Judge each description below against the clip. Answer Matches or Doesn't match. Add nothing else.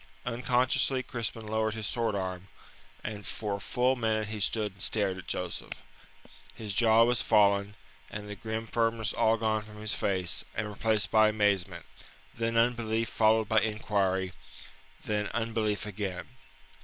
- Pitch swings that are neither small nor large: Doesn't match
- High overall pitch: Doesn't match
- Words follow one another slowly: Doesn't match